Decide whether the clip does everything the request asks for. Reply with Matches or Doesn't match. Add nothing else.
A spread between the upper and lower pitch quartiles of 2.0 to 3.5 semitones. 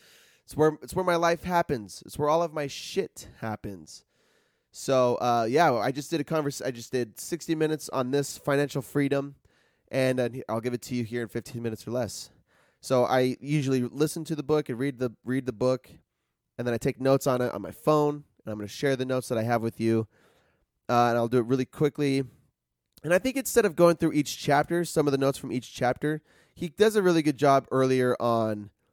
Doesn't match